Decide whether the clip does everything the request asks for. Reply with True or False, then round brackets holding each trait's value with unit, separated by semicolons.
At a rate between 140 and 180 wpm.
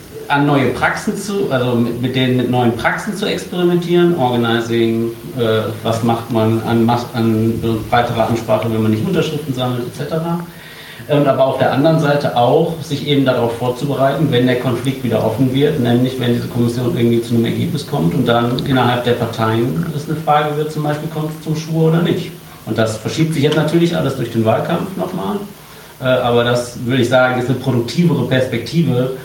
False (190 wpm)